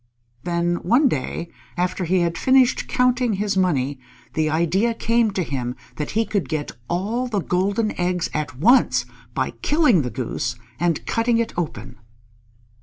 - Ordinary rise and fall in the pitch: No, wide, 6.4 semitones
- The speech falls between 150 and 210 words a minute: Yes, average, 155 wpm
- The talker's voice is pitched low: No, medium, 180 Hz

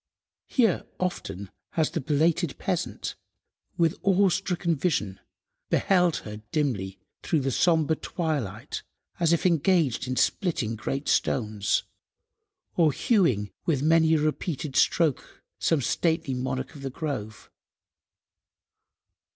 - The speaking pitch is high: No, medium, 155 Hz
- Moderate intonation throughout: Yes, average, 4.9 semitones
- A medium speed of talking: No, slow, 110 wpm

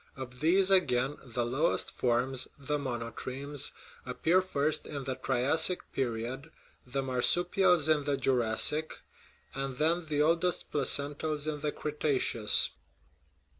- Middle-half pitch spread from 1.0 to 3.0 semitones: No, average, 3.5 semitones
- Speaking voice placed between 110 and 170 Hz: Yes, medium, 140 Hz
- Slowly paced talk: Yes, slow, 120 wpm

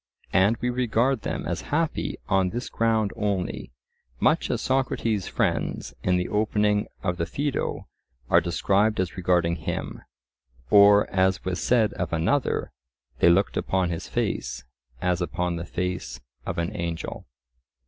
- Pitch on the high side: No, very low, 95 Hz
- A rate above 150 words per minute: No, average, 145 wpm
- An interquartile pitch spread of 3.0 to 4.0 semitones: Yes, average, 3.7 semitones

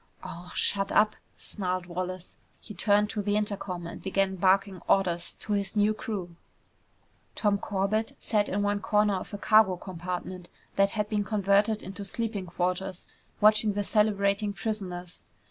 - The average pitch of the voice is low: No, high, 200 Hz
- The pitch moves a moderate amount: No, narrow, 2.2 semitones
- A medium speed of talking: Yes, average, 150 wpm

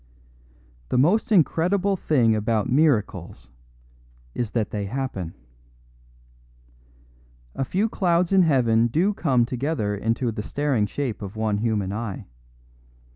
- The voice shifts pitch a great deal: Yes, wide, 7.0 semitones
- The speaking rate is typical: No, slow, 120 wpm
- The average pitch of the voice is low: Yes, low, 120 Hz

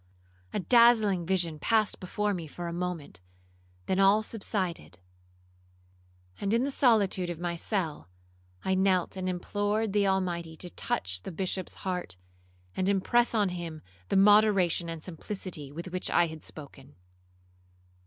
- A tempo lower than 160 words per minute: Yes, average, 145 wpm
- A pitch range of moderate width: Yes, average, 3.2 semitones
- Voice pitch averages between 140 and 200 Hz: Yes, medium, 185 Hz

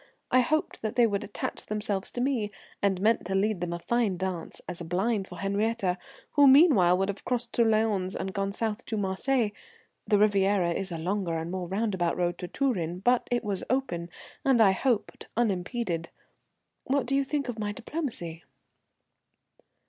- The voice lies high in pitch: Yes, high, 205 Hz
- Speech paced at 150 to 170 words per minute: No, average, 180 wpm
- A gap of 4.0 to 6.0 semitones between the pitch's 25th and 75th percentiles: Yes, average, 4.6 semitones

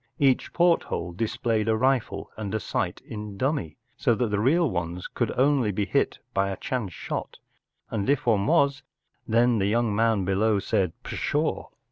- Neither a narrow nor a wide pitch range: Yes, average, 4.4 semitones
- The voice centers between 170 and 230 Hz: No, low, 110 Hz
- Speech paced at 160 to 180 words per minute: Yes, average, 165 wpm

